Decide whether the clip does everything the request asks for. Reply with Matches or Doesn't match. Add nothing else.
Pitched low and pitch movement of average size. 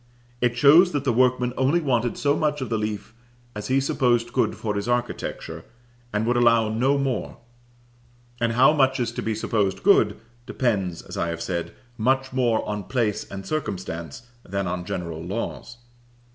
Matches